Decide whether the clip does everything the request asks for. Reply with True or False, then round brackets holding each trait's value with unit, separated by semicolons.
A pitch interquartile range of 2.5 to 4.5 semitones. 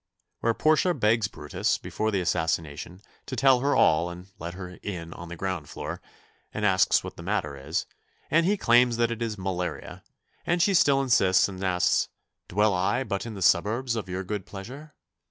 False (5.1 semitones)